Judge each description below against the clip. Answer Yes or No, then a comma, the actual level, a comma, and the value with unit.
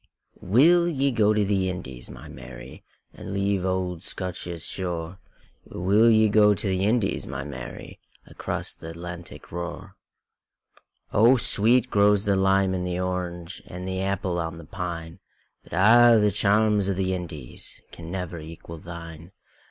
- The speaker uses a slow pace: Yes, slow, 130 wpm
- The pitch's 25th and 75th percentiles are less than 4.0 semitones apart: Yes, average, 3.2 semitones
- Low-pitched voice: Yes, very low, 95 Hz